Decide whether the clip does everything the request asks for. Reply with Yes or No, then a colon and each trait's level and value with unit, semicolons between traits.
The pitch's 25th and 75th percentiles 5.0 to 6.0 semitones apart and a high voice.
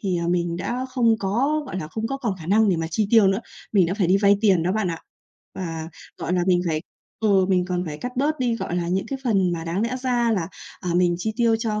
No: average, 4.5 semitones; high, 195 Hz